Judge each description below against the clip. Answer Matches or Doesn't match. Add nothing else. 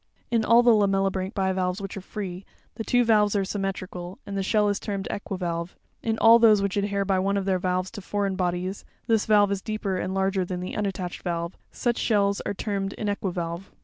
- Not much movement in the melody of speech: Matches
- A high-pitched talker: Matches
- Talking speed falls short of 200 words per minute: Doesn't match